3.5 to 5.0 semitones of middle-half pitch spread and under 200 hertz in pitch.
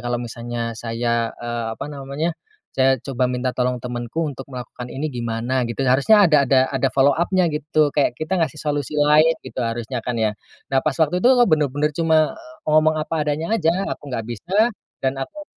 Yes: average, 4.2 semitones; medium, 140 Hz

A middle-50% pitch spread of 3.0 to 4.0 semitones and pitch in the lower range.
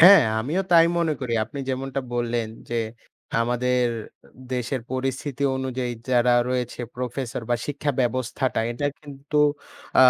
No: narrow, 2.6 semitones; low, 130 Hz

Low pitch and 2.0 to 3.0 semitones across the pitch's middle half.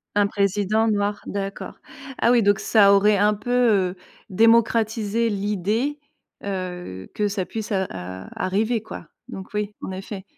No: high, 205 Hz; narrow, 2.4 semitones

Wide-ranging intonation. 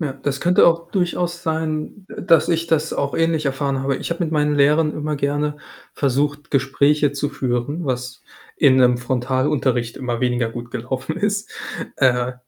No: average, 3.4 semitones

